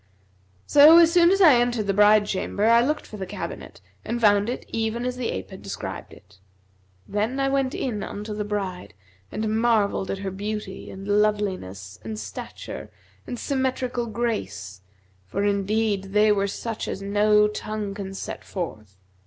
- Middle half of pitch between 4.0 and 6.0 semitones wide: No, average, 3.3 semitones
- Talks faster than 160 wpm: Yes, average, 170 wpm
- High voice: Yes, high, 210 Hz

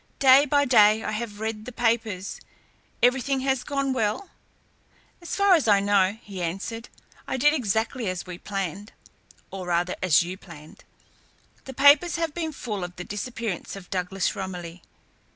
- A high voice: Yes, high, 215 Hz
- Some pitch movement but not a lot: No, wide, 5.9 semitones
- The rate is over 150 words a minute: Yes, average, 160 wpm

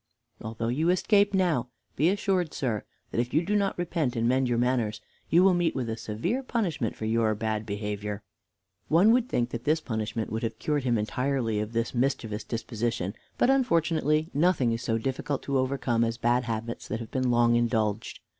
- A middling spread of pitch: No, wide, 5.9 semitones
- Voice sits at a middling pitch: No, low, 120 Hz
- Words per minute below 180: No, average, 190 wpm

